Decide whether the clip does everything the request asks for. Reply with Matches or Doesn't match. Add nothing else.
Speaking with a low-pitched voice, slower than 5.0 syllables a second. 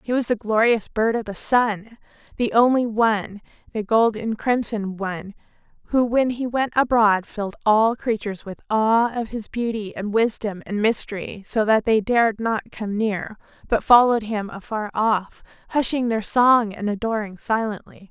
Doesn't match